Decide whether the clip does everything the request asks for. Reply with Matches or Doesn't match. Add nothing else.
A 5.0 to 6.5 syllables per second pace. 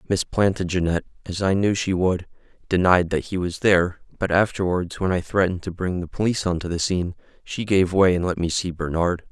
Matches